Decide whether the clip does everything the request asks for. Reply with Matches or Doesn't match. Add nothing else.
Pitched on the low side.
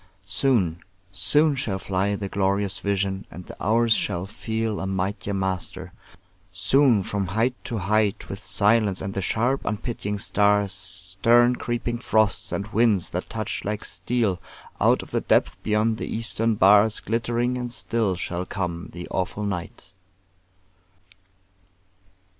Matches